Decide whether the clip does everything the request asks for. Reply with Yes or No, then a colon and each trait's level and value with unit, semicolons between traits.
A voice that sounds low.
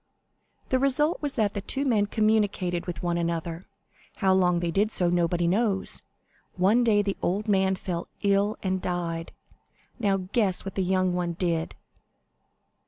No: high, 190 Hz